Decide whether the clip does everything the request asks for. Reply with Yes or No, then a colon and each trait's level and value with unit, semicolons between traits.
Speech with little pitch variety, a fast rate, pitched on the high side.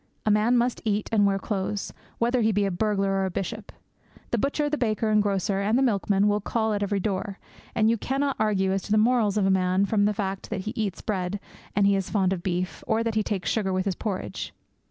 Yes: narrow, 2.2 semitones; fast, 245 wpm; high, 205 Hz